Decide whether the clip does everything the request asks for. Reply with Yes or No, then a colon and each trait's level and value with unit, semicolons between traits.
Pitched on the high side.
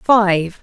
Yes: high, 200 Hz